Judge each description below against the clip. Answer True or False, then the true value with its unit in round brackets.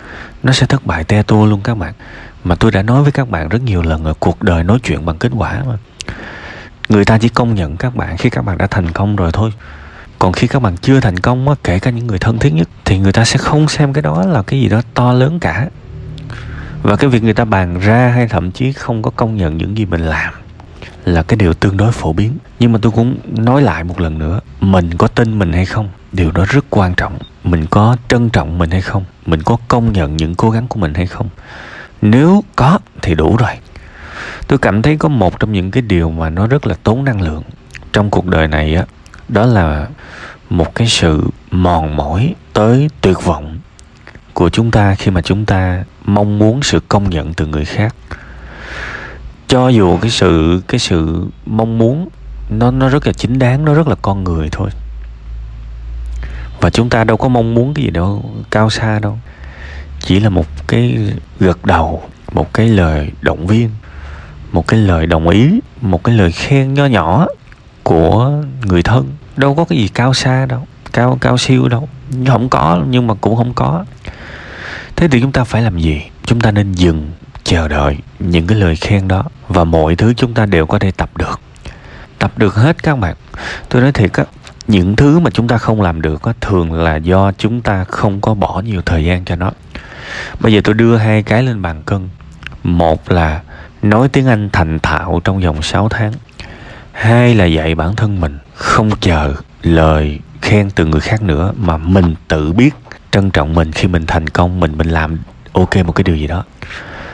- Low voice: True (100 Hz)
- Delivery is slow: False (210 wpm)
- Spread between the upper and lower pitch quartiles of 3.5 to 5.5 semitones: False (5.9 semitones)